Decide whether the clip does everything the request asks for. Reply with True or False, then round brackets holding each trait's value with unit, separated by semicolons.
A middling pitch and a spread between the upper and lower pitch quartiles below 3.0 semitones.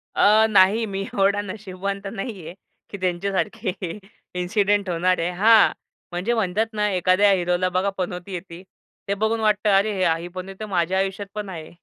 False (195 Hz; 2.4 semitones)